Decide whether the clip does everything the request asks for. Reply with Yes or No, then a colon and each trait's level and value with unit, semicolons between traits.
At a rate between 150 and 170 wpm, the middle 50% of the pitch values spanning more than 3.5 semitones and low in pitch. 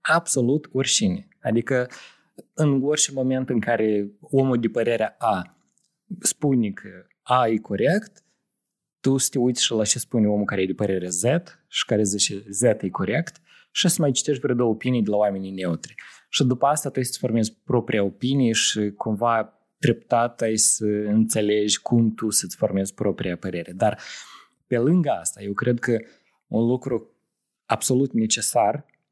Yes: average, 165 wpm; average, 4.1 semitones; low, 115 Hz